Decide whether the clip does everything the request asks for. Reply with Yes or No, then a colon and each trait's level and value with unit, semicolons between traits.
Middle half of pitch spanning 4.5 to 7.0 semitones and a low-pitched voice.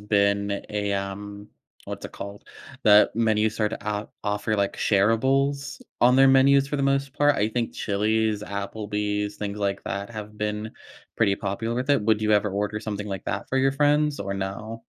No: average, 2.9 semitones; low, 105 Hz